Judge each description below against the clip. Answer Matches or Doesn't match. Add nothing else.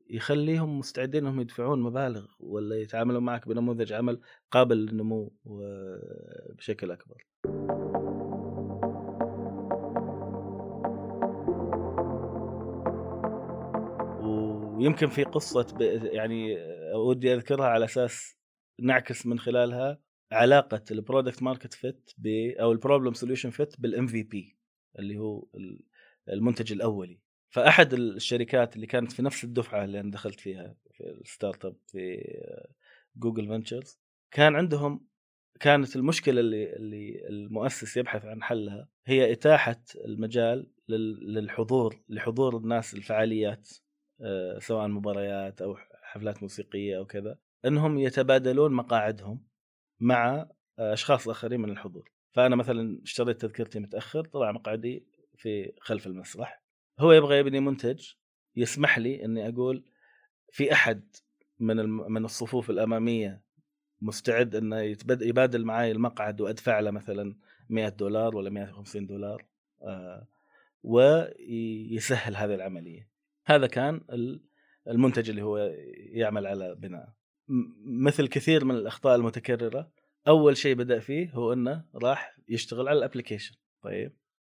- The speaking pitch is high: Doesn't match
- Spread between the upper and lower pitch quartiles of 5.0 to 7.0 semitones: Doesn't match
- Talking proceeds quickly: Doesn't match